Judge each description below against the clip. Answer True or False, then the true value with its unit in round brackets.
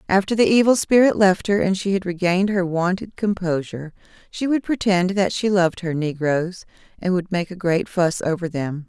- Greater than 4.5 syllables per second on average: True (5.3 syllables/s)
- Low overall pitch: False (185 Hz)